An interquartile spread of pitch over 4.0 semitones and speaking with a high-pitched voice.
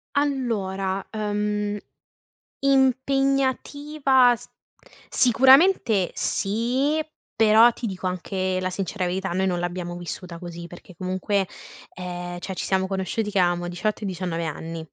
Yes: average, 5.2 semitones; high, 195 Hz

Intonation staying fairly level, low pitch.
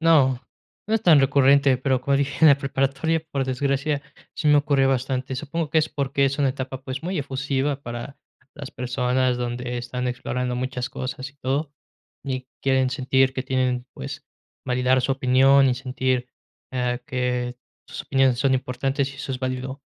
Yes: narrow, 1.6 semitones; low, 130 Hz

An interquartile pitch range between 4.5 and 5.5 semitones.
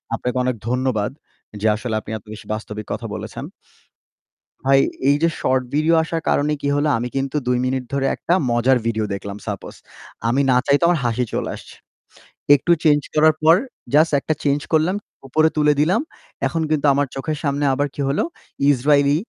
No: average, 3.5 semitones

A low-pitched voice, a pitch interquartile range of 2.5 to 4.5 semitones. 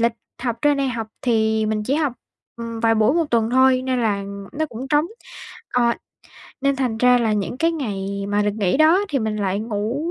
No: high, 235 Hz; average, 3.8 semitones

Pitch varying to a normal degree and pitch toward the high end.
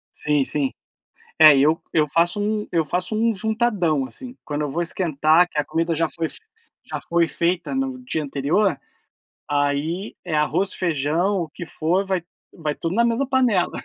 No: average, 4.7 semitones; medium, 170 Hz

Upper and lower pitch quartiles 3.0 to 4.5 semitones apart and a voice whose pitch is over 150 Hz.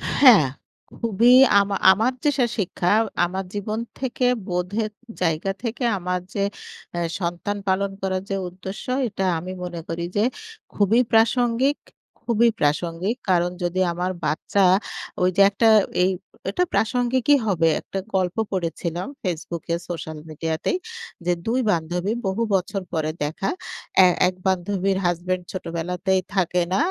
Yes: average, 3.5 semitones; high, 190 Hz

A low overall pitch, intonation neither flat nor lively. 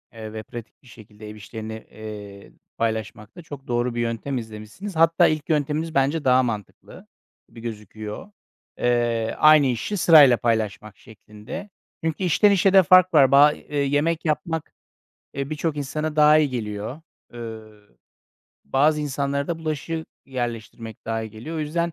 No: low, 130 Hz; wide, 5.8 semitones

